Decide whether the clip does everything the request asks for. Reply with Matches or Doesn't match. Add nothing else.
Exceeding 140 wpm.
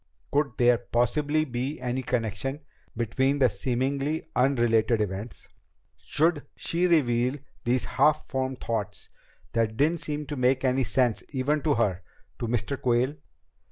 Doesn't match